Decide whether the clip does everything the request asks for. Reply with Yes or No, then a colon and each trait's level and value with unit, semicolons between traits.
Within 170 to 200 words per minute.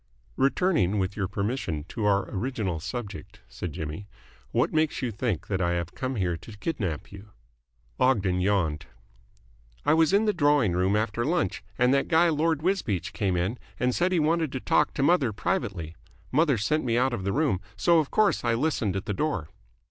Yes: average, 190 wpm